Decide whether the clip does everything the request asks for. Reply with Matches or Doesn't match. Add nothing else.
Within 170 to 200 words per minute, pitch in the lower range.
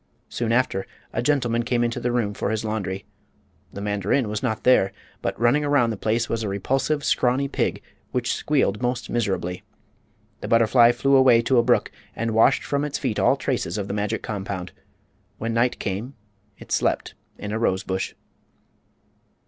Matches